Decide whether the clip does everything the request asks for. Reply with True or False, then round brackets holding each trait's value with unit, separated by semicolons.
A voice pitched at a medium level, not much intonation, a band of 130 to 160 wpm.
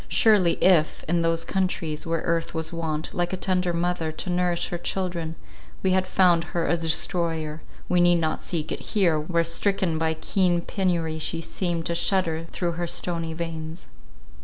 False (170 Hz; 1.7 semitones; 175 wpm)